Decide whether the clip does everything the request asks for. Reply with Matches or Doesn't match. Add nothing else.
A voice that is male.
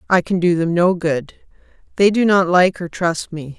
Doesn't match